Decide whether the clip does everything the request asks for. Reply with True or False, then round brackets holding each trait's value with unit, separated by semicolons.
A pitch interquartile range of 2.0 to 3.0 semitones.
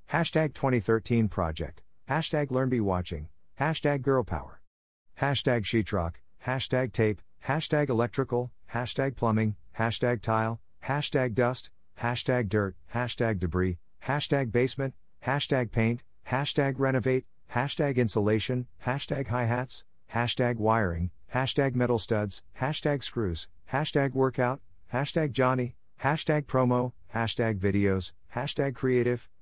False (3.7 semitones)